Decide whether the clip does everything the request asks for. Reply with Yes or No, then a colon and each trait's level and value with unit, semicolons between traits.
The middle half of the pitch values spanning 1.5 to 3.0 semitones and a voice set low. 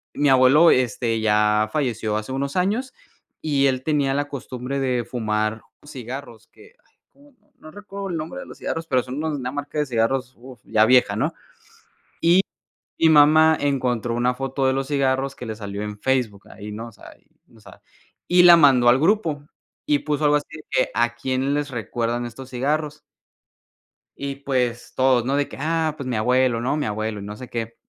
No: average, 3.7 semitones; low, 130 Hz